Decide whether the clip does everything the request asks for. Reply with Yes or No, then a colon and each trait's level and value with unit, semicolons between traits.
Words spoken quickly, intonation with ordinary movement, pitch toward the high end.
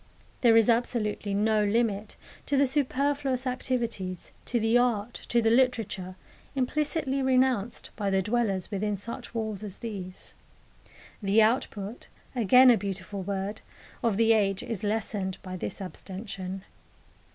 No: slow, 135 wpm; average, 3.8 semitones; high, 220 Hz